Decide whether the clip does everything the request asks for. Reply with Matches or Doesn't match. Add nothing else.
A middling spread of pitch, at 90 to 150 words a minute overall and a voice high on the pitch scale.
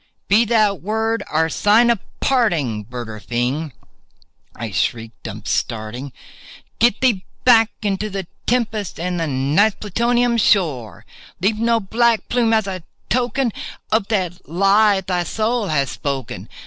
Doesn't match